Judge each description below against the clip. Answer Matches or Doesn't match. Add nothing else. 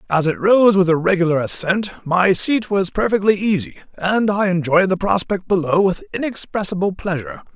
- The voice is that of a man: Matches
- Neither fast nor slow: Matches